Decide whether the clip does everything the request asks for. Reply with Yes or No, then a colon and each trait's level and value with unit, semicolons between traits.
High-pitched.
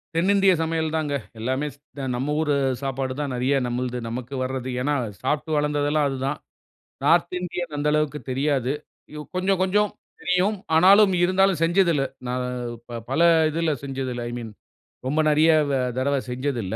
No: medium, 150 Hz